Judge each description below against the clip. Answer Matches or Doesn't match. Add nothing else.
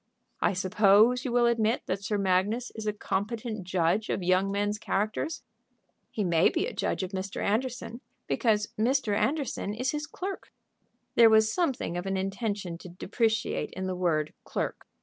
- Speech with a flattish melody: Doesn't match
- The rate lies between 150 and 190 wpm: Matches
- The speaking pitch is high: Matches